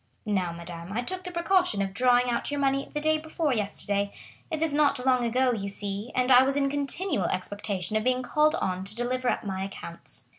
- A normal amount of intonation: No, wide, 6.2 semitones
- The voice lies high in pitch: Yes, very high, 250 Hz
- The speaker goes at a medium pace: No, fast, 215 wpm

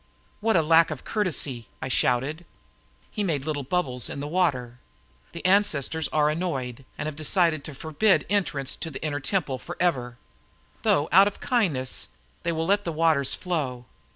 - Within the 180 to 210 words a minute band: No, average, 160 wpm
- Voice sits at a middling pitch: Yes, medium, 155 Hz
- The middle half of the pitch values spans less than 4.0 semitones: No, average, 4.8 semitones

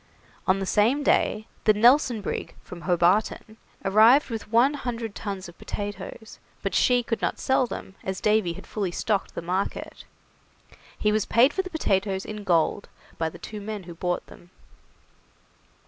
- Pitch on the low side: No, high, 210 Hz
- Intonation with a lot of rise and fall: No, average, 3.4 semitones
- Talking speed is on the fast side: No, average, 165 wpm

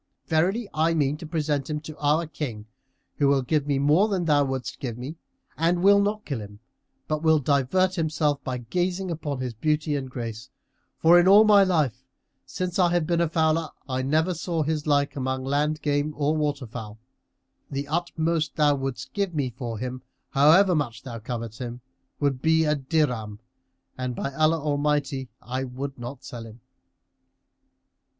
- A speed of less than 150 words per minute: No, average, 175 wpm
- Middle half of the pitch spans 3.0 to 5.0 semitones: Yes, average, 3.8 semitones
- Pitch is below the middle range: No, medium, 145 Hz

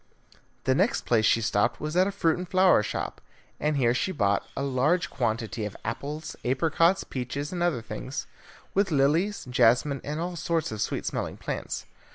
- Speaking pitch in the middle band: Yes, medium, 145 Hz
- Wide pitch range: Yes, wide, 6.3 semitones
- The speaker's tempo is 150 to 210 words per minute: Yes, average, 180 wpm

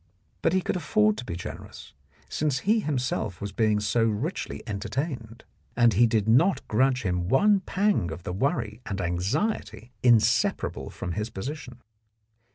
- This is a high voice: No, low, 120 Hz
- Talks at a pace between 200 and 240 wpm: No, average, 155 wpm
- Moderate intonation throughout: No, wide, 6.2 semitones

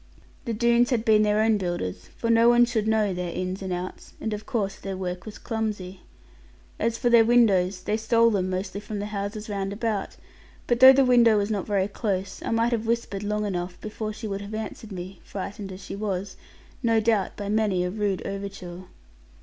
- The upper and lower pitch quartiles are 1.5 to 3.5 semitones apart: Yes, average, 2.8 semitones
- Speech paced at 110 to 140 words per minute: No, fast, 205 wpm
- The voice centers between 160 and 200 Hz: No, high, 210 Hz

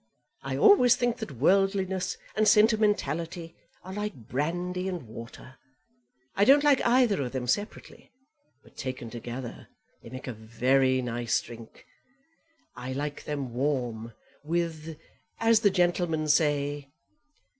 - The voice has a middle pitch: Yes, medium, 155 Hz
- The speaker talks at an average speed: No, slow, 125 wpm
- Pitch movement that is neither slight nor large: No, wide, 7.2 semitones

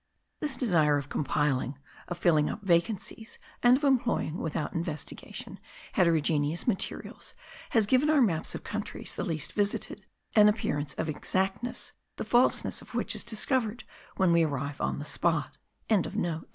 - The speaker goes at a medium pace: Yes, average, 145 wpm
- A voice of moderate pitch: Yes, medium, 175 Hz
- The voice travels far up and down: Yes, wide, 6.8 semitones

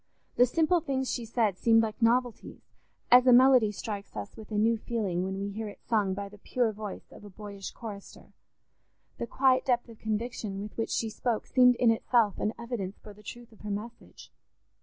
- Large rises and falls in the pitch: No, average, 2.8 semitones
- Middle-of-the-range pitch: No, high, 225 Hz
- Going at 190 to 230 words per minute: Yes, average, 200 wpm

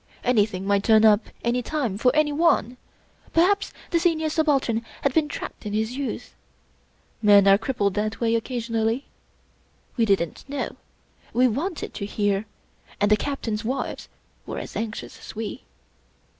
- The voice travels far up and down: No, average, 4.9 semitones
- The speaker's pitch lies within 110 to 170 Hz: No, high, 230 Hz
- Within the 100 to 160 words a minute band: Yes, average, 145 wpm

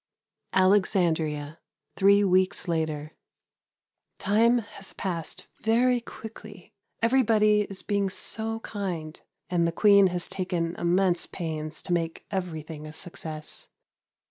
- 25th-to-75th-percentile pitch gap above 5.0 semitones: No, average, 3.9 semitones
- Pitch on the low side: No, medium, 185 Hz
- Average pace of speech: No, slow, 110 wpm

